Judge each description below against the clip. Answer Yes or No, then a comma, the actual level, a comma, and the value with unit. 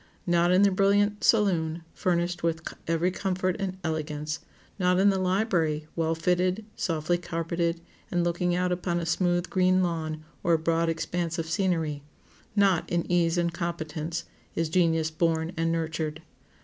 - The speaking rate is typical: Yes, average, 150 wpm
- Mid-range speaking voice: Yes, medium, 170 Hz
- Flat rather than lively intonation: Yes, narrow, 2.0 semitones